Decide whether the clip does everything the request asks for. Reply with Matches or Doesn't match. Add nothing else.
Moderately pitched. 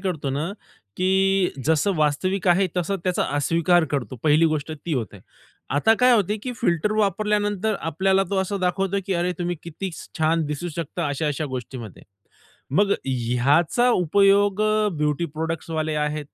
Matches